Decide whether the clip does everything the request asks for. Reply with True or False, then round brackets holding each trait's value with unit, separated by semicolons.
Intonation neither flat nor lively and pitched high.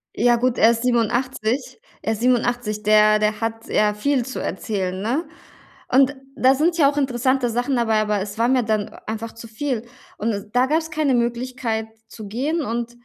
True (3.0 semitones; 235 Hz)